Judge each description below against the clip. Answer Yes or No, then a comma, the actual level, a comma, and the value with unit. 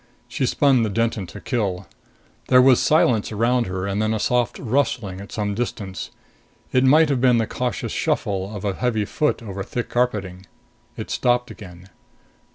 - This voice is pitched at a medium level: No, low, 115 Hz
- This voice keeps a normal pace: Yes, average, 170 wpm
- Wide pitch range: No, average, 3.9 semitones